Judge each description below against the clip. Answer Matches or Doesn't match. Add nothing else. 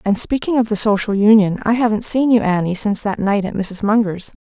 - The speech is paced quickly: Matches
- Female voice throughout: Matches